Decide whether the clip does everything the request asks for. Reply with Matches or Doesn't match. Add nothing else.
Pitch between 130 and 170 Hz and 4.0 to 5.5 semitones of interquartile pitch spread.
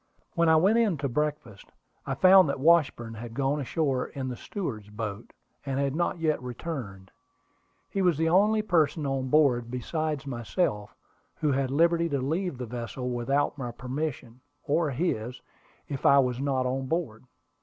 Matches